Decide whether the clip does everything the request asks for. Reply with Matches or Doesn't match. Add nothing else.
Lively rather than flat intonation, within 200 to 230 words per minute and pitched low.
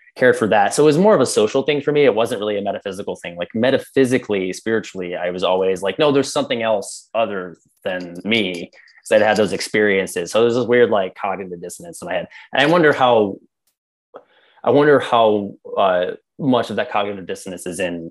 Matches